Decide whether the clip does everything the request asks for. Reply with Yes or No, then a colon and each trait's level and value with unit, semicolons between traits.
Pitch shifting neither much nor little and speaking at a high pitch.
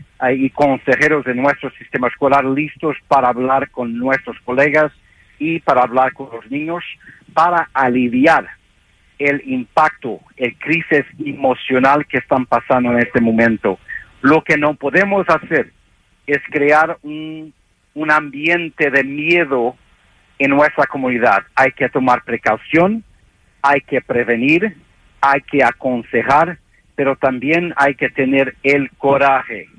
No: average, 3.1 semitones; medium, 140 Hz